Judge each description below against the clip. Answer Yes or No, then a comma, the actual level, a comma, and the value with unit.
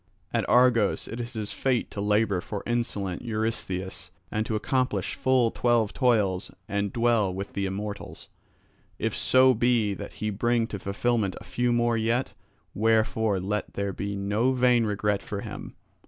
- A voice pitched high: No, low, 110 Hz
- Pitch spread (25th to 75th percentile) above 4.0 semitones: No, average, 2.9 semitones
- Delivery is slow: No, average, 160 wpm